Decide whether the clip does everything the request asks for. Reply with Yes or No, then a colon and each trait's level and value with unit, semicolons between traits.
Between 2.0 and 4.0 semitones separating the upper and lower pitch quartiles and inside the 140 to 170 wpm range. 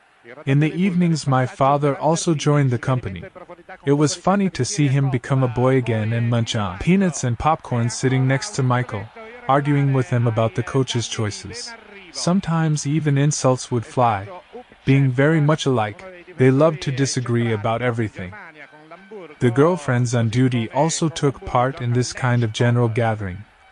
No: average, 4.4 semitones; average, 160 wpm